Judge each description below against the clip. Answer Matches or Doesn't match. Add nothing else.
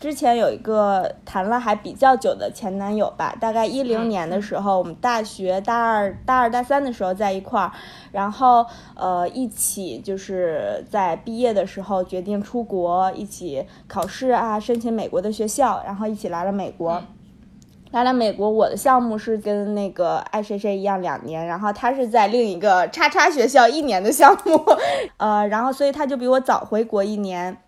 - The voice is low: Doesn't match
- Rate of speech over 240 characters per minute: Matches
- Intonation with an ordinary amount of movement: Matches